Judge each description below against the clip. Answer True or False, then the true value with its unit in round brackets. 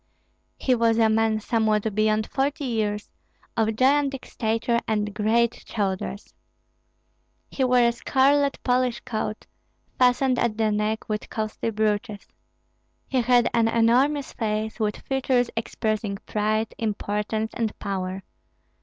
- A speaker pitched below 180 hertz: False (225 Hz)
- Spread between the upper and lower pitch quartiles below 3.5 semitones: True (2.5 semitones)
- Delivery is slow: True (125 wpm)